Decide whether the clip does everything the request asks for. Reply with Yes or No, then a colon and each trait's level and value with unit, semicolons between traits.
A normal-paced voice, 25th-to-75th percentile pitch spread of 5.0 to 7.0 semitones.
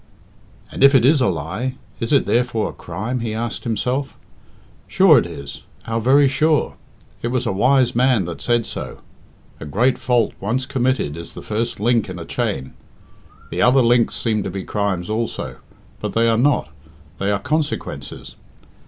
No: average, 175 wpm; average, 4.1 semitones